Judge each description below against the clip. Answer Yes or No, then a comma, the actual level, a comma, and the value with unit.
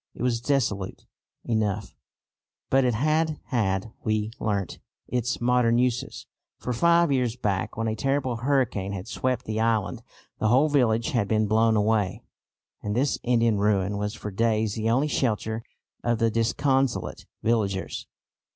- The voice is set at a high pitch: No, low, 115 Hz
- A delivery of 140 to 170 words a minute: Yes, average, 150 wpm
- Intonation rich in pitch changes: No, average, 2.9 semitones